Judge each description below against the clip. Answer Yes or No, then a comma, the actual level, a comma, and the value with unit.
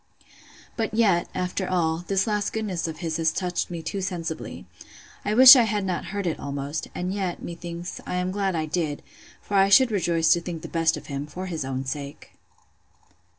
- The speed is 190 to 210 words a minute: Yes, average, 195 wpm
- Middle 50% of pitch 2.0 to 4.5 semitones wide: Yes, average, 3.5 semitones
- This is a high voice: No, medium, 175 Hz